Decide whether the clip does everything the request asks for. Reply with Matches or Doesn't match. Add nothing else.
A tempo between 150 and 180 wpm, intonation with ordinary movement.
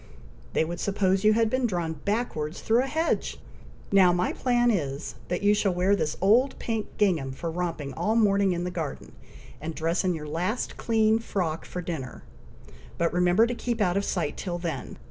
Doesn't match